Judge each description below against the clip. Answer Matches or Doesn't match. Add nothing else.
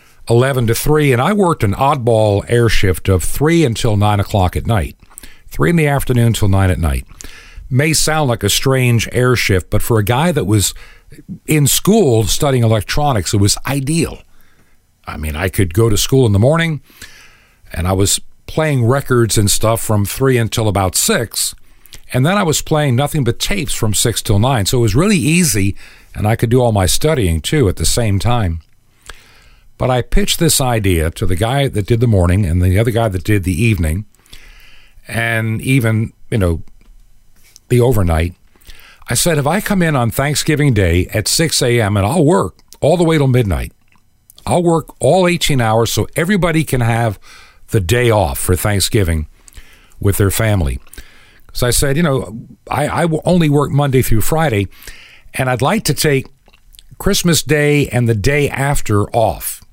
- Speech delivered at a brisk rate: Doesn't match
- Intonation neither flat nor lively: Doesn't match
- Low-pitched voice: Matches